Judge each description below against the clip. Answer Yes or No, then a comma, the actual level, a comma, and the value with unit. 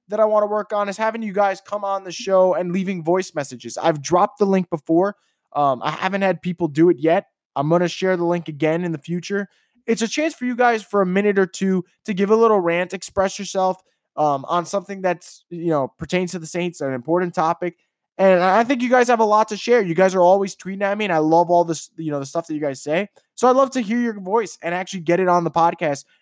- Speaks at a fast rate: Yes, fast, 265 wpm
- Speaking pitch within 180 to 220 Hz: Yes, medium, 185 Hz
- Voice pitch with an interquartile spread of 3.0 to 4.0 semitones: Yes, average, 3.3 semitones